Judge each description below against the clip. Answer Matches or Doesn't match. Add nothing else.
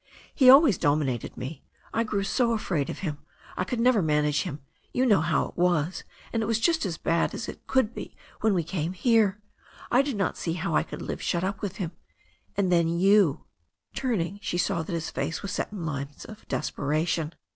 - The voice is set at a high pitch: Doesn't match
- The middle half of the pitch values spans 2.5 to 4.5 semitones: Doesn't match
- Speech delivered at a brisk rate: Matches